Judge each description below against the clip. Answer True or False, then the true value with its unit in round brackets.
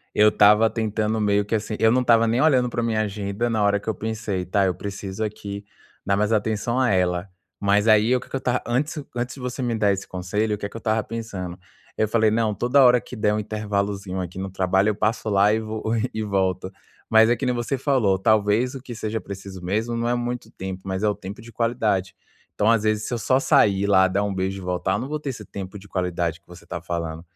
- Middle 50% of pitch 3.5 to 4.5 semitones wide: False (3.0 semitones)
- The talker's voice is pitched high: False (105 Hz)